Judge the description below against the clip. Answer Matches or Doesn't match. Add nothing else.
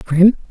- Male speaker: Doesn't match